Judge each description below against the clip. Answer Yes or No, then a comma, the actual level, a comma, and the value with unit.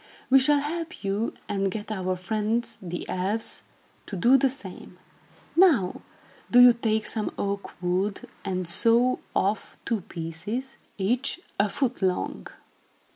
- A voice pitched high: Yes, high, 215 Hz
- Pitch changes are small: No, average, 4.7 semitones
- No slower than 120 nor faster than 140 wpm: Yes, slow, 135 wpm